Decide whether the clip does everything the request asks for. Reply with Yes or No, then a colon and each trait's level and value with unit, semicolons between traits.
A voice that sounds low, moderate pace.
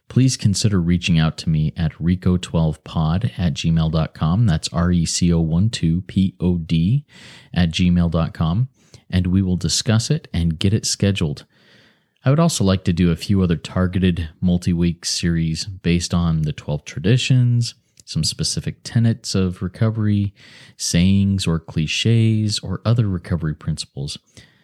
Yes: very low, 90 Hz; average, 150 wpm